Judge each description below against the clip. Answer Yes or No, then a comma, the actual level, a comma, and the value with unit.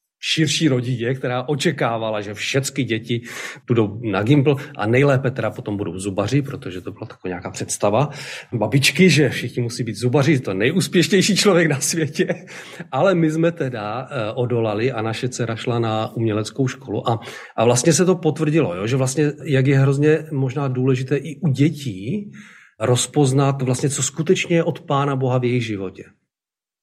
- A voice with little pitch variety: No, average, 4.6 semitones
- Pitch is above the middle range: No, low, 135 Hz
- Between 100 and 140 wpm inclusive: No, average, 165 wpm